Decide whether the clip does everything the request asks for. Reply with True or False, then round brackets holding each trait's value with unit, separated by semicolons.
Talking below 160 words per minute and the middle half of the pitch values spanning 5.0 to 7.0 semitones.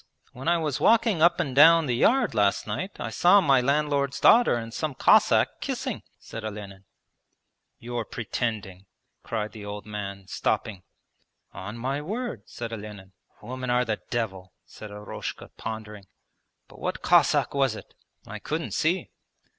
True (150 wpm; 5.6 semitones)